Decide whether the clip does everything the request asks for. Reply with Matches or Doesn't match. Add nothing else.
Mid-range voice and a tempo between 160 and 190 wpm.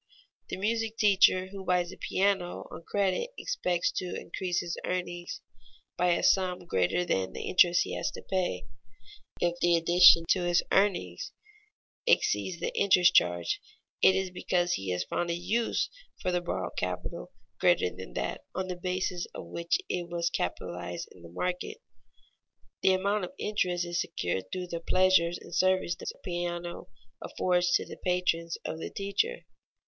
Matches